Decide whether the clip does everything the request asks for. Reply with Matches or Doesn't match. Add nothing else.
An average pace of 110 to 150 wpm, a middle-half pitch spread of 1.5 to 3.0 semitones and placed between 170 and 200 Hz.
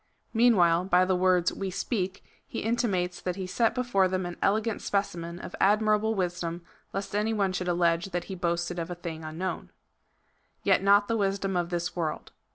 Doesn't match